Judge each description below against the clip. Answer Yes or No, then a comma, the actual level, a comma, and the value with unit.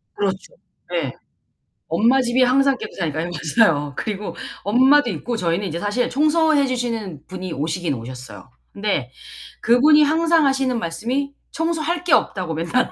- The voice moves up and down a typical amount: No, wide, 8.3 semitones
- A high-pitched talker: Yes, high, 230 Hz